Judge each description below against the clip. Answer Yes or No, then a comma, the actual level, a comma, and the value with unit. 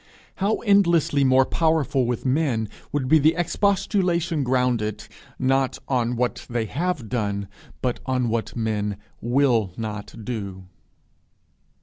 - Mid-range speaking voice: No, low, 130 Hz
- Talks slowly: Yes, slow, 115 wpm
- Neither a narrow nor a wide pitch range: No, wide, 5.8 semitones